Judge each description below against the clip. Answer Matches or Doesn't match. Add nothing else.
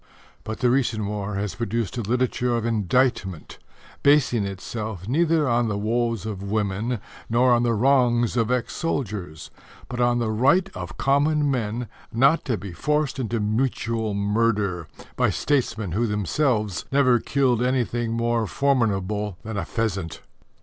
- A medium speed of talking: Matches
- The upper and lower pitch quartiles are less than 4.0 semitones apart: Matches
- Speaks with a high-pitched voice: Doesn't match